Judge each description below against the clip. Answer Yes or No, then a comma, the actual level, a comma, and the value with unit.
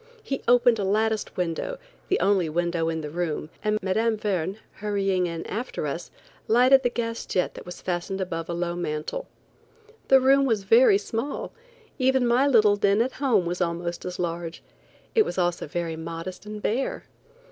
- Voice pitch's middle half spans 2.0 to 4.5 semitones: No, average, 5.2 semitones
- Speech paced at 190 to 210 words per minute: No, average, 175 wpm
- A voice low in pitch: No, high, 195 Hz